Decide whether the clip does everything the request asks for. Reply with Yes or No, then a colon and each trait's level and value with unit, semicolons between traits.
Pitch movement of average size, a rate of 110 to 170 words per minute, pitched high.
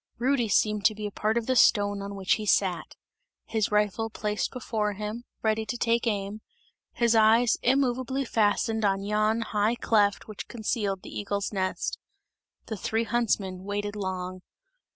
No: narrow, 2.1 semitones; average, 160 wpm; high, 215 Hz